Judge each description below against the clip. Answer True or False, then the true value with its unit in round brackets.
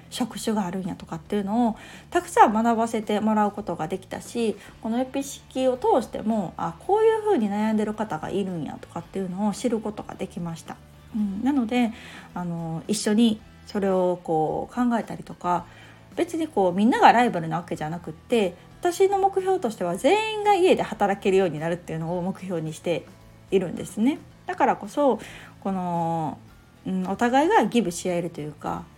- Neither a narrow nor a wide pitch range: False (5.7 semitones)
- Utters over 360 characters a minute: True (380 characters per minute)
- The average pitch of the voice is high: True (205 Hz)